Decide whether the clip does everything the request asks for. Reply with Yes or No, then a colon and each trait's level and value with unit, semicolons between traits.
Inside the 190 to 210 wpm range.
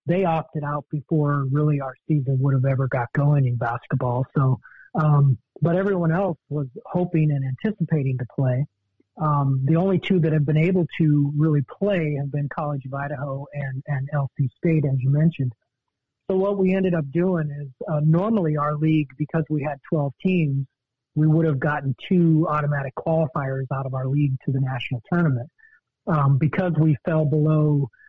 No: average, 180 wpm